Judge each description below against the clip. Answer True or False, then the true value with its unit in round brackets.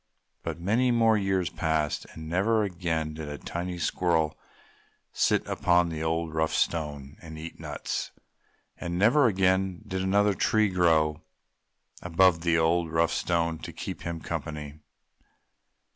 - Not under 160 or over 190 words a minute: False (140 wpm)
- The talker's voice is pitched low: True (85 Hz)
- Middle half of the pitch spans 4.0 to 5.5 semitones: False (2.9 semitones)